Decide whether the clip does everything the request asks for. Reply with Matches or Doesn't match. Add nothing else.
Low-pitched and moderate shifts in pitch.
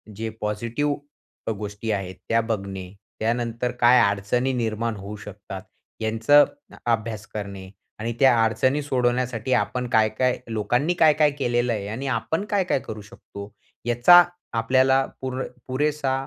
Matches